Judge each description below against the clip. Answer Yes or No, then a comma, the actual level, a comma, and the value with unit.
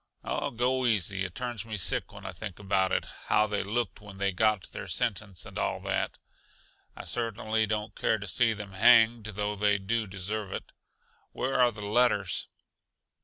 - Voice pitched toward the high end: No, low, 105 Hz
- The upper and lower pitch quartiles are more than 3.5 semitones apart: No, narrow, 2.5 semitones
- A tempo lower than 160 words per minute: No, average, 180 wpm